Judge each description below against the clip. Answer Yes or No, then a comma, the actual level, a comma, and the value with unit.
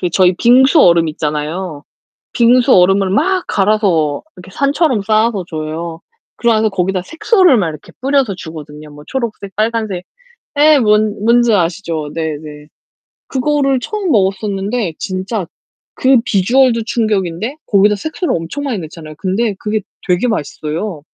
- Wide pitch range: Yes, wide, 6.1 semitones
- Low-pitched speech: No, high, 200 Hz